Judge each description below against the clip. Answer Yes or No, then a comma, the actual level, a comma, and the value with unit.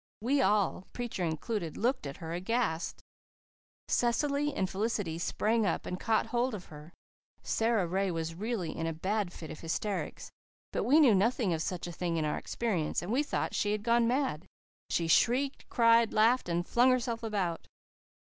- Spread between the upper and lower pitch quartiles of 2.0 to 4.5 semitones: No, wide, 5.6 semitones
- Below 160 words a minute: No, average, 180 wpm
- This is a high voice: Yes, high, 210 Hz